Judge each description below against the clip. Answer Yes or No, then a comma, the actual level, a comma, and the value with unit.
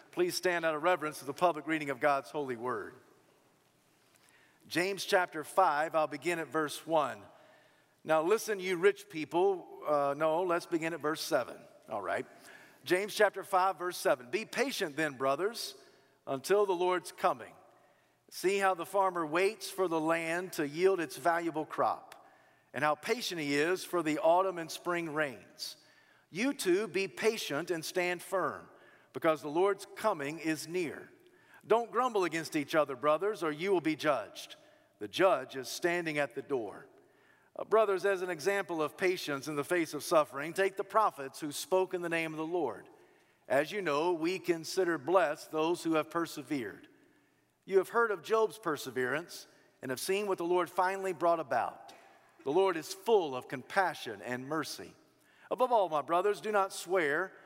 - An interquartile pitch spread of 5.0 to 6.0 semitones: No, average, 3.9 semitones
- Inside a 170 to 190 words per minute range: Yes, average, 175 wpm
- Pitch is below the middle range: No, medium, 175 Hz